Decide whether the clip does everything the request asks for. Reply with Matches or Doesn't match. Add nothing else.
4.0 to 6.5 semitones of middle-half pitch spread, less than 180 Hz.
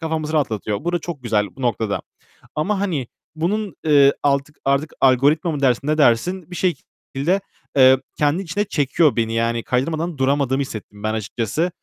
Matches